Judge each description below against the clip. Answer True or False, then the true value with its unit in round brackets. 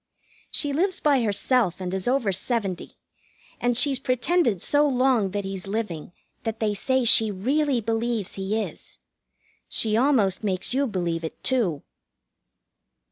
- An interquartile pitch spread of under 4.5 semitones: False (5.2 semitones)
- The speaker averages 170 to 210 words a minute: False (140 wpm)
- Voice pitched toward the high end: True (225 Hz)